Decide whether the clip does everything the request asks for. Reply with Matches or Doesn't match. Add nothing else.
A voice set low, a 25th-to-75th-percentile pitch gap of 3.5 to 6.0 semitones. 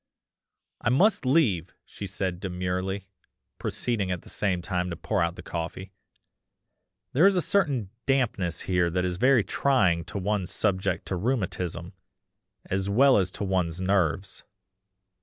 Matches